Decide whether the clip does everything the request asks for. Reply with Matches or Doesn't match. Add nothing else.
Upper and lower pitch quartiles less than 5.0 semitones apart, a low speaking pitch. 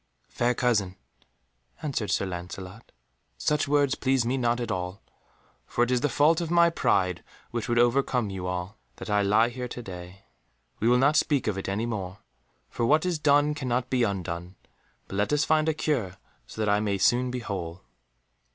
Doesn't match